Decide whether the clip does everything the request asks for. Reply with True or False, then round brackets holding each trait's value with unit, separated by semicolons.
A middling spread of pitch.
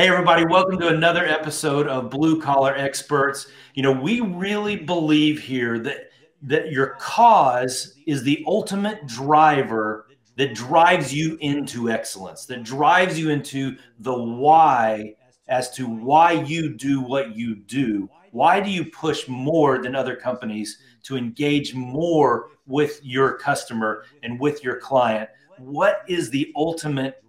True (3.9 semitones)